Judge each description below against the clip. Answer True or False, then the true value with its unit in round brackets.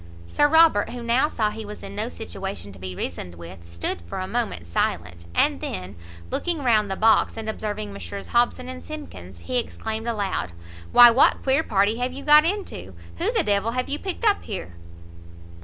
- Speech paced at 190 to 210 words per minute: True (195 wpm)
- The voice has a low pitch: False (215 Hz)